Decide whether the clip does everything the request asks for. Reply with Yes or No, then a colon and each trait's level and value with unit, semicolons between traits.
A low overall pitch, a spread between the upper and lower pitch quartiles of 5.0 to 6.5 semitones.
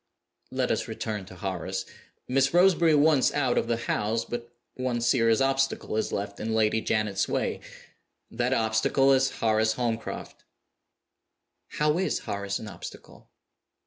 No: low, 115 Hz; average, 3.8 semitones